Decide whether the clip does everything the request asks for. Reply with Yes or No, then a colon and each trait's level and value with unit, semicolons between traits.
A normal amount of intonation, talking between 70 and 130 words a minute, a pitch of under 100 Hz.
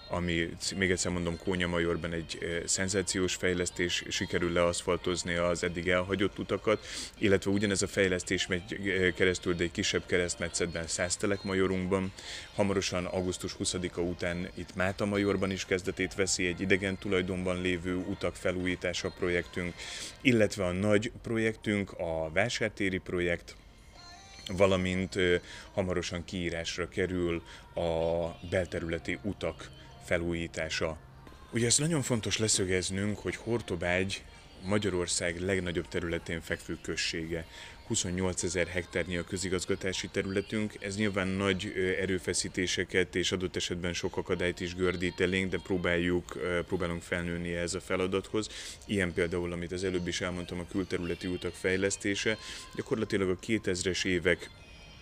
No: narrow, 1.9 semitones; average, 120 wpm; very low, 90 Hz